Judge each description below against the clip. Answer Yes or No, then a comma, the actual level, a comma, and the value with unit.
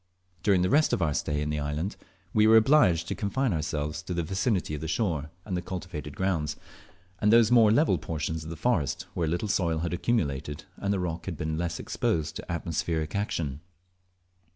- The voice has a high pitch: No, very low, 85 Hz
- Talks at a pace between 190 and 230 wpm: Yes, average, 200 wpm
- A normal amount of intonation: Yes, average, 4.6 semitones